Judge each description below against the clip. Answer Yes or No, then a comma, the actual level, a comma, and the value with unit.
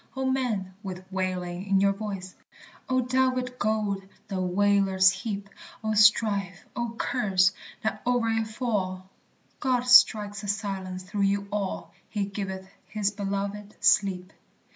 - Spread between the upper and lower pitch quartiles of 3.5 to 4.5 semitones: No, narrow, 2.4 semitones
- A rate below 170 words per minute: Yes, slow, 135 wpm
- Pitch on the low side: No, high, 200 Hz